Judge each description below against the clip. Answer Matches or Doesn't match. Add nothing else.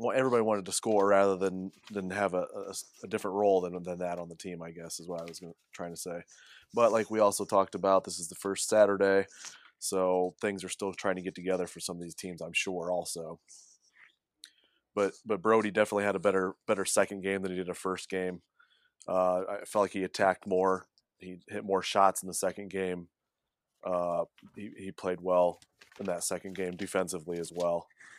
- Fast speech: Matches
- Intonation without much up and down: Matches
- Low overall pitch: Matches